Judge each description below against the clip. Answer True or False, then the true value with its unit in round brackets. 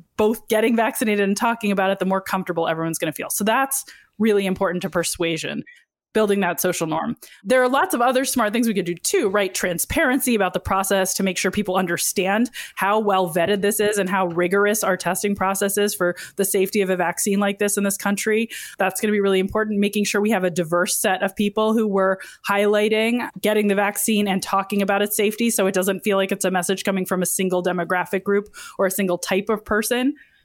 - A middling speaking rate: False (225 wpm)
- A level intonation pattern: True (2.2 semitones)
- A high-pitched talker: True (200 Hz)